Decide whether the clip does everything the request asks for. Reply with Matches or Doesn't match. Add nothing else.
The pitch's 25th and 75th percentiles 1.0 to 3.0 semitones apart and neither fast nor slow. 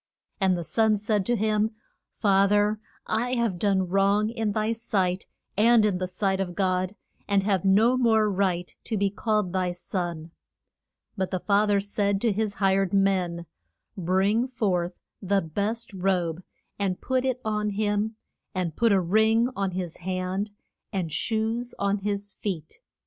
Matches